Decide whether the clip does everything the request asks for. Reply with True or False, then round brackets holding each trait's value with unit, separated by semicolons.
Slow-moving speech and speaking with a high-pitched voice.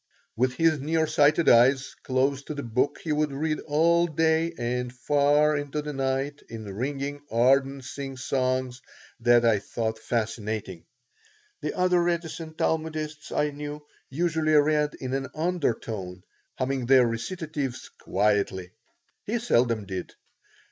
False (130 wpm; 140 Hz)